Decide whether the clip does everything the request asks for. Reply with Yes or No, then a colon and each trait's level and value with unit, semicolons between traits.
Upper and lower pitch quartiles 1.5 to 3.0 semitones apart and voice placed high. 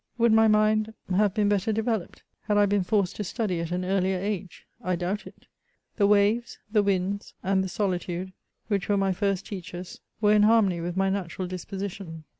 Yes: narrow, 2.4 semitones; high, 195 Hz